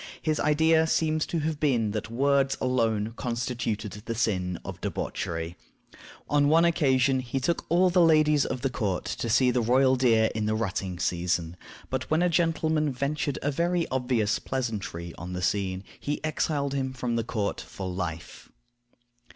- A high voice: No, low, 130 Hz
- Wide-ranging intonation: Yes, wide, 5.9 semitones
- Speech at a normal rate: Yes, average, 165 wpm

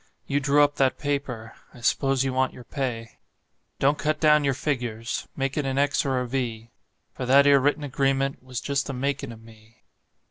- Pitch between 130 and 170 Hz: Yes, low, 135 Hz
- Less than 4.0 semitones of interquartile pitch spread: Yes, narrow, 2.4 semitones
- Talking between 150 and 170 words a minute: No, average, 200 wpm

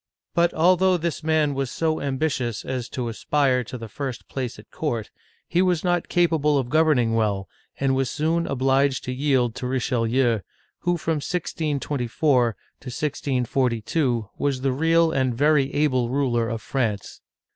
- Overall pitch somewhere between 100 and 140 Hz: Yes, low, 135 Hz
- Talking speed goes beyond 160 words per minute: No, average, 155 wpm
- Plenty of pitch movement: No, average, 4.1 semitones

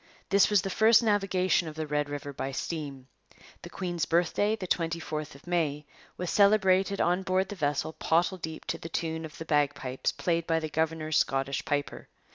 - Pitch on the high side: No, medium, 165 Hz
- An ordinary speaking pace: Yes, average, 185 wpm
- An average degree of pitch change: Yes, average, 3.9 semitones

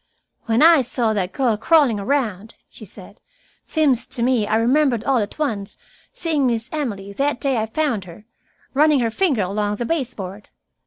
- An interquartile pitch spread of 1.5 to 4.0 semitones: No, average, 5.1 semitones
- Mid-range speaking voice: No, high, 240 Hz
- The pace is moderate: Yes, average, 170 wpm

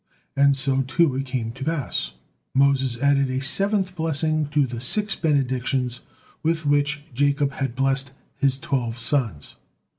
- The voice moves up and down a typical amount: No, narrow, 2.2 semitones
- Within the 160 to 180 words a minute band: No, average, 145 wpm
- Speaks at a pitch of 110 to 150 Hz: Yes, low, 135 Hz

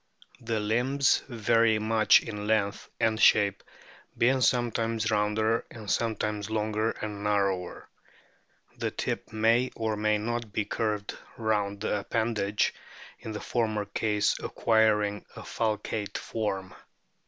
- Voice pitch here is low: Yes, low, 110 Hz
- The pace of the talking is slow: Yes, slow, 120 wpm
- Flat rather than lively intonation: Yes, narrow, 1.5 semitones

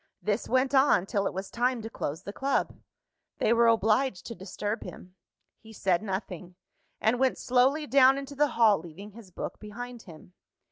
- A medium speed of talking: Yes, average, 180 wpm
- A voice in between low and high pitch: No, high, 225 Hz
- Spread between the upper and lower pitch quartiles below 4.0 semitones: No, average, 4.8 semitones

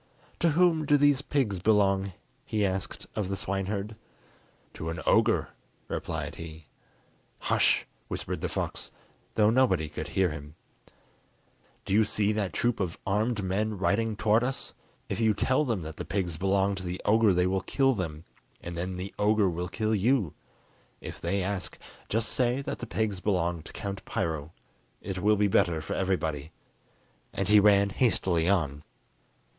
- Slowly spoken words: No, average, 165 wpm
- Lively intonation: No, average, 3.4 semitones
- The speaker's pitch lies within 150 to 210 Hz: No, low, 100 Hz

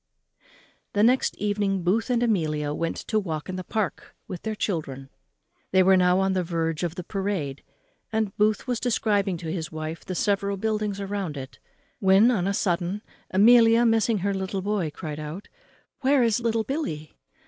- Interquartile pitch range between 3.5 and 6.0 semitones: Yes, average, 4.2 semitones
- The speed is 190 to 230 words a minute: No, average, 175 wpm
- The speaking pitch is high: Yes, high, 195 Hz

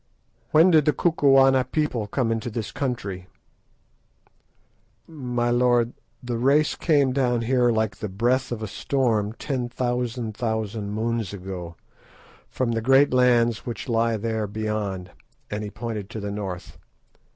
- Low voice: Yes, low, 115 Hz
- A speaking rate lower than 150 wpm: Yes, average, 140 wpm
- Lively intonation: No, average, 3.1 semitones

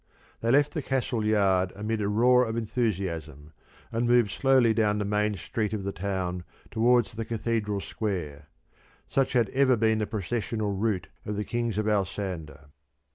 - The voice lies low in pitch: Yes, low, 105 Hz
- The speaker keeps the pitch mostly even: No, average, 3.1 semitones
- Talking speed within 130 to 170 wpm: Yes, average, 165 wpm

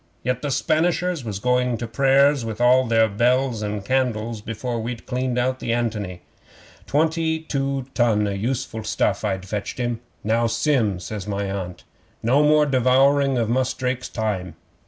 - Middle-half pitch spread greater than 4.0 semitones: No, average, 3.7 semitones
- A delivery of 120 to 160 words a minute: Yes, average, 155 wpm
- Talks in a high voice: No, low, 120 Hz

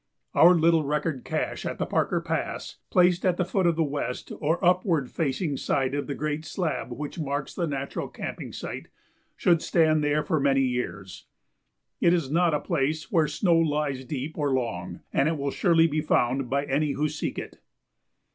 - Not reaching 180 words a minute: No, average, 185 wpm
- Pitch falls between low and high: Yes, medium, 150 Hz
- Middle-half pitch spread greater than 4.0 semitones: No, average, 3.2 semitones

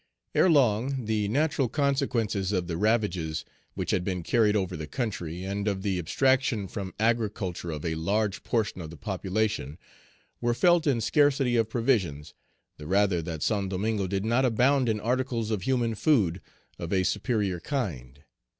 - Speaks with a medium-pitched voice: No, low, 105 Hz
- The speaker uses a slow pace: No, average, 160 wpm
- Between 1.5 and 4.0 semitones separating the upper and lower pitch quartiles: No, average, 4.8 semitones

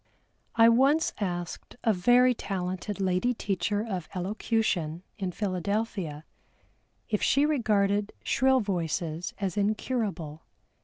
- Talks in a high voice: Yes, high, 200 Hz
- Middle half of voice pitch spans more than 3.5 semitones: Yes, average, 4.0 semitones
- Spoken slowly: Yes, slow, 105 wpm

